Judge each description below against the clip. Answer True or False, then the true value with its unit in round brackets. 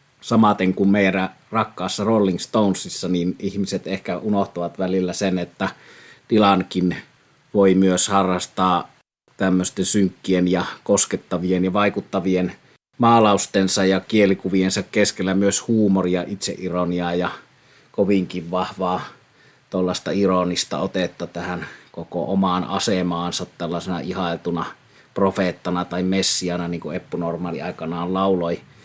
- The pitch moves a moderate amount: False (1.6 semitones)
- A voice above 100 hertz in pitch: False (95 Hz)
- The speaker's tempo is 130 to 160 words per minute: False (105 wpm)